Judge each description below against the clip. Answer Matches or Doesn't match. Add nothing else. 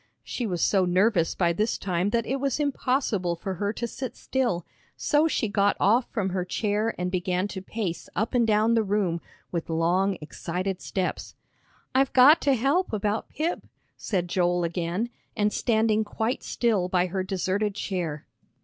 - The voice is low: Doesn't match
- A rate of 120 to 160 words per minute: Doesn't match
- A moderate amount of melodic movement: Matches